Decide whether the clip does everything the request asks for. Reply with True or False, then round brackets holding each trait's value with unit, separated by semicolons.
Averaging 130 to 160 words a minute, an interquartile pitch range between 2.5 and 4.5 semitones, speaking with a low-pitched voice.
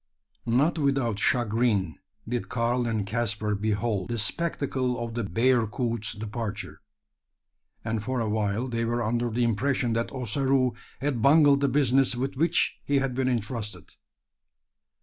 True (140 wpm; 3.1 semitones; 120 Hz)